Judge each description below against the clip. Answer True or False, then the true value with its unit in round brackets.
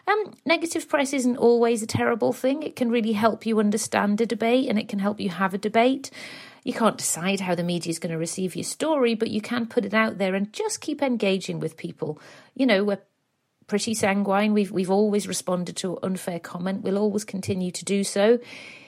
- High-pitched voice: True (210 Hz)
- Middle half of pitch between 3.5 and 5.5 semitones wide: True (4.2 semitones)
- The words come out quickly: True (215 wpm)